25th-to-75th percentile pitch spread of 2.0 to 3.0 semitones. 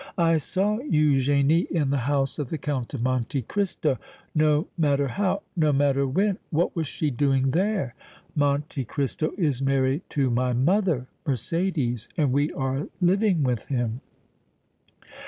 No: average, 3.9 semitones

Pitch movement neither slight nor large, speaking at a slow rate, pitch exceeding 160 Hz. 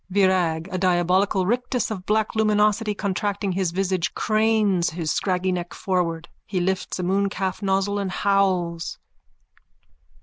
No: narrow, 2.2 semitones; slow, 130 wpm; high, 190 Hz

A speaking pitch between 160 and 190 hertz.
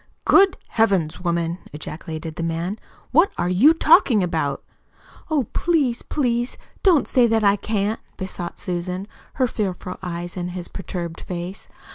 Yes: medium, 185 Hz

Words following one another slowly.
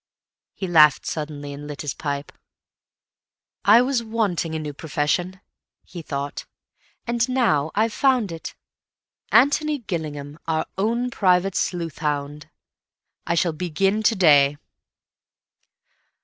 Yes: slow, 115 wpm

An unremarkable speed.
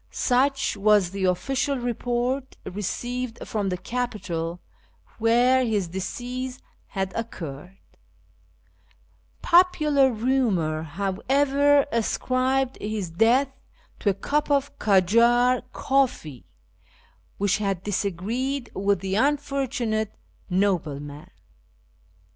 No: slow, 95 wpm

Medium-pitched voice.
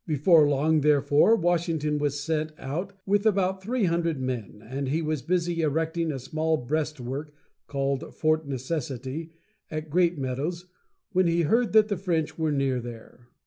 Yes: medium, 155 Hz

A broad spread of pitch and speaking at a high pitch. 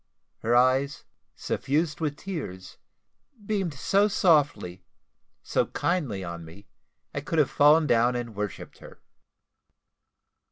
No: wide, 7.5 semitones; medium, 140 Hz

